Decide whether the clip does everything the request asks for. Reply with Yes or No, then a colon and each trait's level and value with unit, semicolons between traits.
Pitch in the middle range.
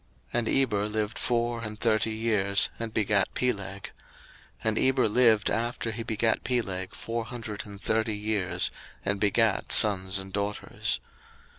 No: low, 110 Hz